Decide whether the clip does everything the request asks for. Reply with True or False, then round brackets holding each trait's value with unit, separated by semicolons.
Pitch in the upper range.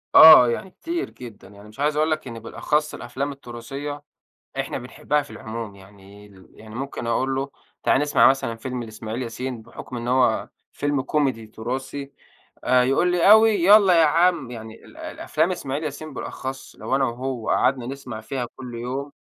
False (130 Hz)